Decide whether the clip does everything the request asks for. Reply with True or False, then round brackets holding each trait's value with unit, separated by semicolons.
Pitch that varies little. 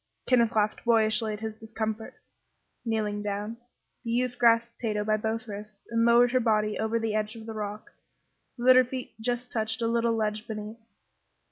True (1.6 semitones)